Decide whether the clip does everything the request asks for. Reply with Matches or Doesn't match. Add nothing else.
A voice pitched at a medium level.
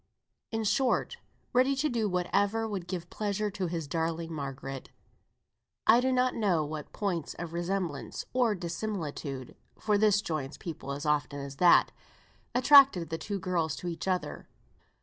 Matches